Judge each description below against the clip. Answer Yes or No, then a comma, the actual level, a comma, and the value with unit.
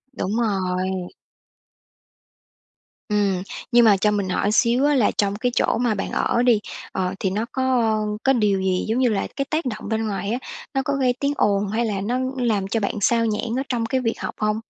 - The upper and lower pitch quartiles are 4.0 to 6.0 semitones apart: No, average, 3.5 semitones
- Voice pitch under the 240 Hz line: Yes, high, 220 Hz